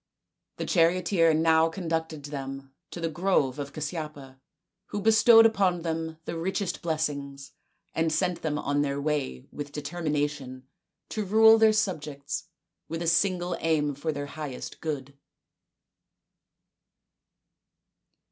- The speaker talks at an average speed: No, slow, 125 wpm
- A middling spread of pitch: Yes, average, 3.4 semitones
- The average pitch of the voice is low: No, medium, 160 Hz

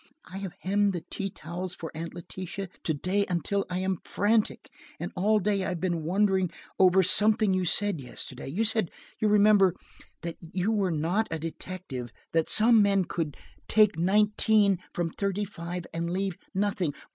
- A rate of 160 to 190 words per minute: Yes, average, 170 wpm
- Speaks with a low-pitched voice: No, medium, 185 Hz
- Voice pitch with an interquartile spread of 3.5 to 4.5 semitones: No, average, 3.1 semitones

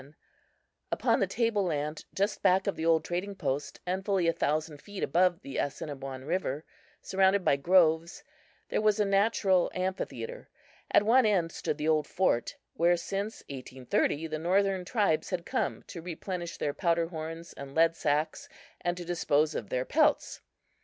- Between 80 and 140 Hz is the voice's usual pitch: No, medium, 170 Hz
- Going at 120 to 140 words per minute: No, average, 165 wpm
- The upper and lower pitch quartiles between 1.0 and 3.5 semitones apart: No, average, 3.9 semitones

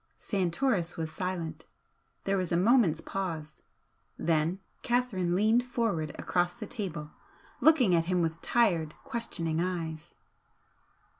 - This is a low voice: No, medium, 180 Hz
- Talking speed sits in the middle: No, slow, 120 wpm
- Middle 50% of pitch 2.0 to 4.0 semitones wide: No, average, 4.7 semitones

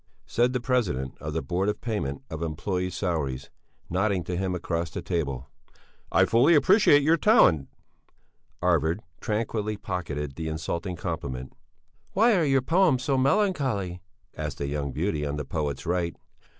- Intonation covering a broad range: Yes, wide, 7.9 semitones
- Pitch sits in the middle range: No, very low, 90 Hz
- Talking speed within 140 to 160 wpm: Yes, average, 150 wpm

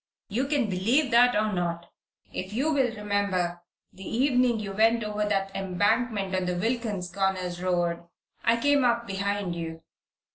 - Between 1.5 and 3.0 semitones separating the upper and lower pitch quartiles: No, average, 4.3 semitones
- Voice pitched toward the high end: Yes, high, 205 Hz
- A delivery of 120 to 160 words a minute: Yes, average, 155 wpm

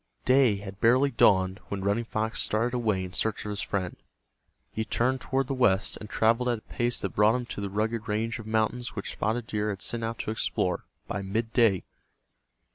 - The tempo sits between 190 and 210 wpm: Yes, average, 200 wpm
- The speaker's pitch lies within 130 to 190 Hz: No, low, 110 Hz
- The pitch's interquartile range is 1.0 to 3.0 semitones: Yes, average, 2.7 semitones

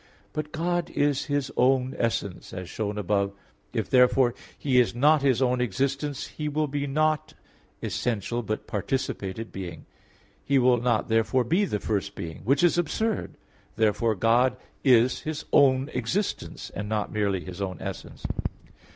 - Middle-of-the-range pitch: No, low, 125 Hz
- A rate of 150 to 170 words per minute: Yes, average, 160 wpm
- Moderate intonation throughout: Yes, average, 4.9 semitones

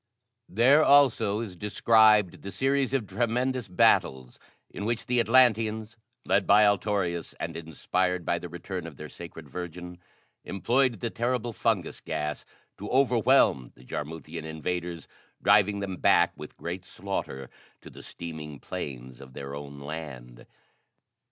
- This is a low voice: Yes, very low, 95 Hz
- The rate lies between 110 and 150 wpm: Yes, average, 140 wpm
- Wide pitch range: Yes, wide, 6.1 semitones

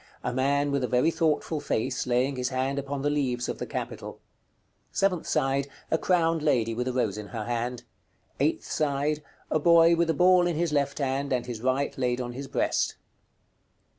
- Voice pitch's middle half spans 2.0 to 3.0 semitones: No, average, 3.5 semitones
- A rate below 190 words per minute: No, average, 195 wpm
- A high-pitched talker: No, medium, 140 Hz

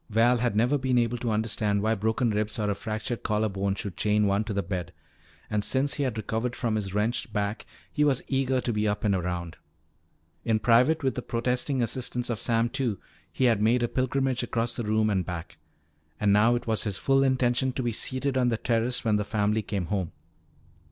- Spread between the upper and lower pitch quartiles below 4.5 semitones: Yes, average, 3.0 semitones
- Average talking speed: No, fast, 215 wpm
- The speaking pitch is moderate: No, low, 115 Hz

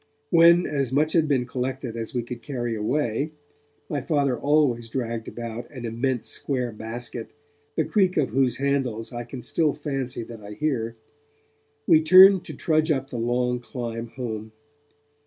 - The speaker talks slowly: No, average, 160 wpm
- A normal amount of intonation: Yes, average, 4.0 semitones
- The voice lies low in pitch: Yes, low, 125 Hz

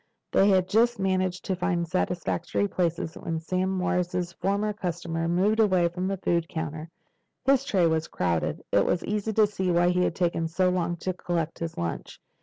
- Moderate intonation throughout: No, narrow, 2.2 semitones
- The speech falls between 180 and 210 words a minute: Yes, average, 190 wpm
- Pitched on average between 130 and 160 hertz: No, medium, 180 Hz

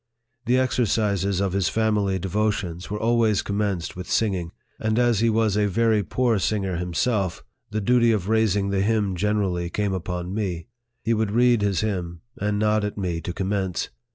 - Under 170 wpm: No, average, 175 wpm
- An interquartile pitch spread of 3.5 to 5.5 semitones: No, average, 2.8 semitones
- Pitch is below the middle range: Yes, low, 105 Hz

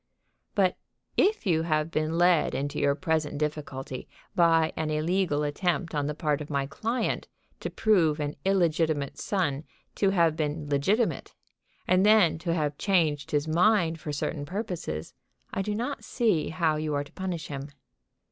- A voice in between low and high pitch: Yes, medium, 160 Hz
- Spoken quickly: No, average, 160 wpm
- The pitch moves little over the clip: No, average, 3.7 semitones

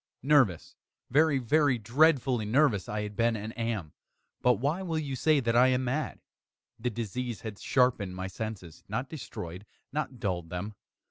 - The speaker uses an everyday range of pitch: Yes, average, 4.7 semitones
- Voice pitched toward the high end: No, low, 120 Hz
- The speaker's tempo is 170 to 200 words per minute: No, average, 160 wpm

